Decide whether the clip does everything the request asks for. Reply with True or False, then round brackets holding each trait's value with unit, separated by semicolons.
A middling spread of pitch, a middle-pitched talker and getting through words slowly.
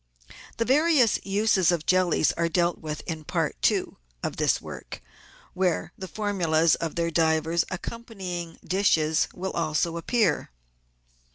True (3.3 semitones; 175 Hz; 130 wpm)